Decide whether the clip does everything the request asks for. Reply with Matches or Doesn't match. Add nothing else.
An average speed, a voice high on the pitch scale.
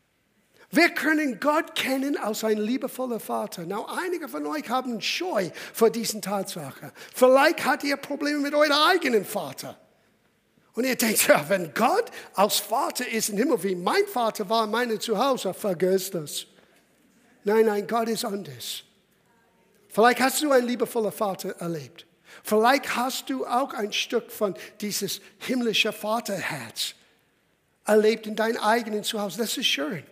Matches